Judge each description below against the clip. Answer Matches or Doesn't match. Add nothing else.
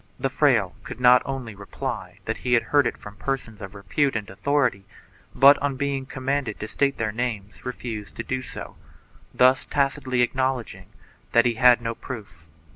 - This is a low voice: Matches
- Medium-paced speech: Matches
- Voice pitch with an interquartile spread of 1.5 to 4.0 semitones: Matches